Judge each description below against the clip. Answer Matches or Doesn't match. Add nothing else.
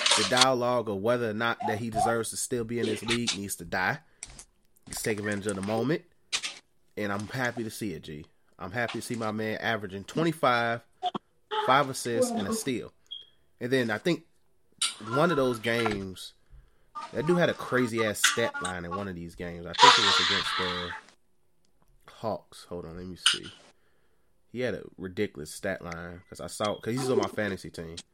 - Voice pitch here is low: Matches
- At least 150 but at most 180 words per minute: Doesn't match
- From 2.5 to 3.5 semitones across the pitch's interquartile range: Doesn't match